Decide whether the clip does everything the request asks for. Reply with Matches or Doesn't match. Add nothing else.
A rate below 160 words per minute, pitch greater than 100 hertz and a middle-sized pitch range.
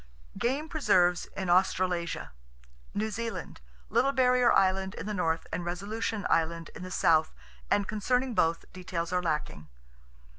Matches